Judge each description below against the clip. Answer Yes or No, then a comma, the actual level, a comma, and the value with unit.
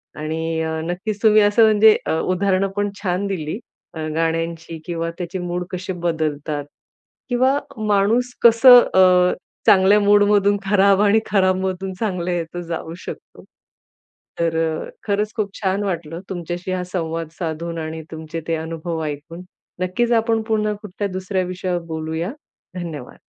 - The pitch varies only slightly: No, average, 3.6 semitones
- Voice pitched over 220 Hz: No, medium, 185 Hz